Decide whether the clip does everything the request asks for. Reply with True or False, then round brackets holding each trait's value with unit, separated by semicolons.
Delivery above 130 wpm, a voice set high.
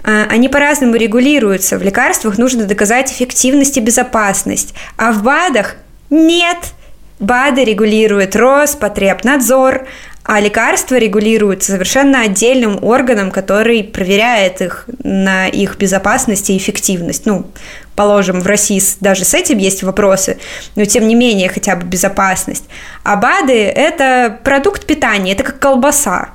False (125 wpm; 225 Hz)